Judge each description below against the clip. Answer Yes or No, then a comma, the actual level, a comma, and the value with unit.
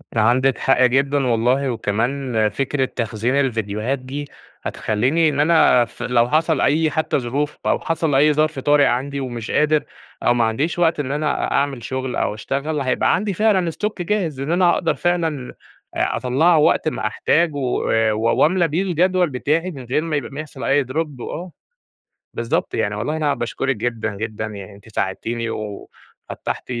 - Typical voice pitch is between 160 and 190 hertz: No, low, 135 Hz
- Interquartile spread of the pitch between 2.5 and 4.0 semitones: No, average, 4.6 semitones